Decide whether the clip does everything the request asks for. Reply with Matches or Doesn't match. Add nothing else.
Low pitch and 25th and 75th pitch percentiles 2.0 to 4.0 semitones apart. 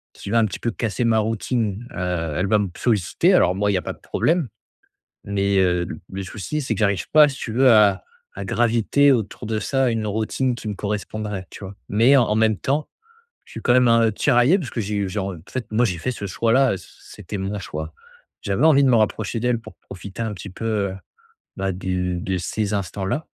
Matches